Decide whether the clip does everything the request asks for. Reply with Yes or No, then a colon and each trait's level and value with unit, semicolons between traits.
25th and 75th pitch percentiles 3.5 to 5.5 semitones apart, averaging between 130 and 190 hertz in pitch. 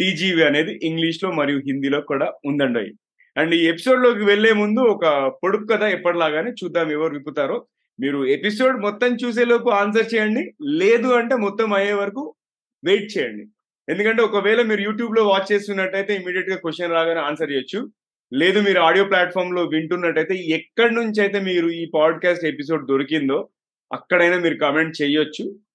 Yes: average, 5.1 semitones; medium, 185 Hz